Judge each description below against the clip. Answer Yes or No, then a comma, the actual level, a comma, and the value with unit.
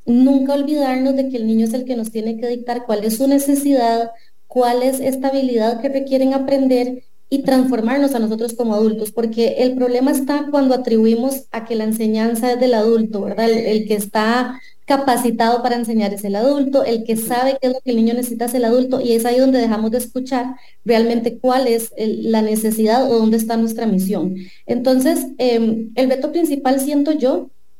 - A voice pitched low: No, high, 245 Hz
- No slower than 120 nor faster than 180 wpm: No, average, 200 wpm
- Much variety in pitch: No, narrow, 2.6 semitones